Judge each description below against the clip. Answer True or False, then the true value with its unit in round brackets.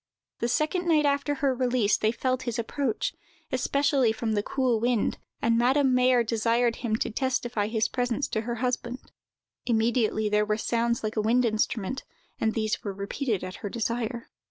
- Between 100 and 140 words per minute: False (175 wpm)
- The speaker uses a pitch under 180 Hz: False (235 Hz)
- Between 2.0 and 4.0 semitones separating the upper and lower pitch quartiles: True (2.7 semitones)